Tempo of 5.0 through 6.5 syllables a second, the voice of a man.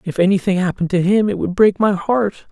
Yes: 5.8 syllables/s; male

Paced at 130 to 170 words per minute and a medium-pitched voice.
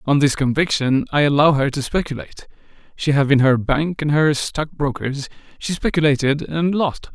Yes: average, 160 wpm; medium, 145 Hz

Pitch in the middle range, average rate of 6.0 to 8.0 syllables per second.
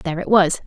Yes: medium, 180 Hz; 6.6 syllables/s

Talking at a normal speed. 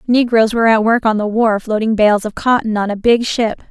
No: fast, 245 wpm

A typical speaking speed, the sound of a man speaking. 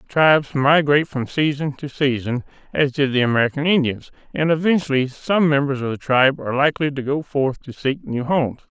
Yes: average, 185 wpm; male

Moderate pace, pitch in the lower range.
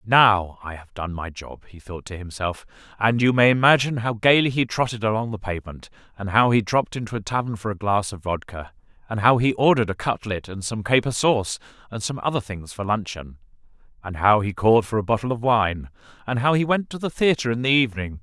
No: fast, 225 wpm; low, 110 Hz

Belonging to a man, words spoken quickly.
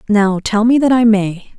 No: female; fast, 225 wpm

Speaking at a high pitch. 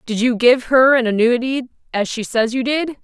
Yes: high, 245 Hz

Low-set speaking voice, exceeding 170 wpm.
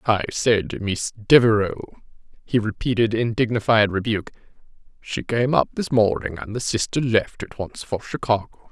No: low, 110 Hz; average, 150 wpm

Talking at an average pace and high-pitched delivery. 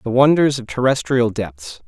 No: average, 160 wpm; low, 120 Hz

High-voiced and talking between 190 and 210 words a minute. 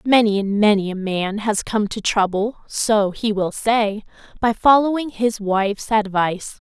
No: high, 210 Hz; average, 145 wpm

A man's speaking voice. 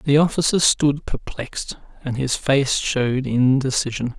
Yes: male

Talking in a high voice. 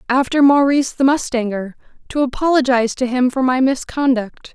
Yes: very high, 260 Hz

